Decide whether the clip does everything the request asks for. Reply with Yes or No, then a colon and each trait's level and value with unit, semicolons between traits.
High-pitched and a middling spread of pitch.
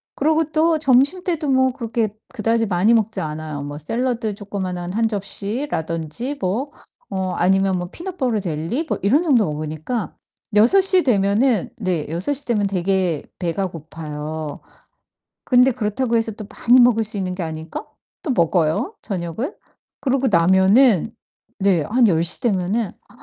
No: high, 205 Hz; wide, 6.2 semitones